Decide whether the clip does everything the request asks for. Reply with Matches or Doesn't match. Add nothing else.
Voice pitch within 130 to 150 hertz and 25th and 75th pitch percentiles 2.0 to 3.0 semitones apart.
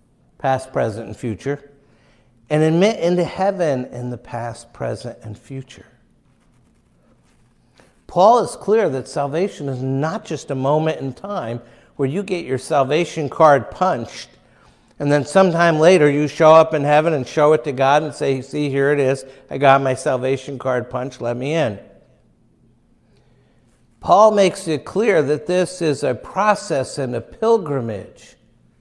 Doesn't match